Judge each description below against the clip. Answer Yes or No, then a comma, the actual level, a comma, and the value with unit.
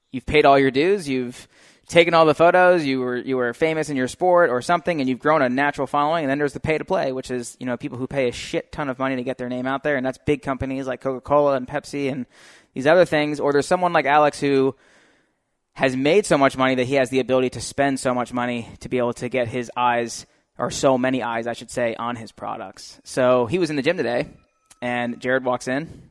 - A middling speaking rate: No, fast, 255 wpm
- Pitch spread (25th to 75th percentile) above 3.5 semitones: No, average, 2.7 semitones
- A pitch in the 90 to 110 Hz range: No, low, 135 Hz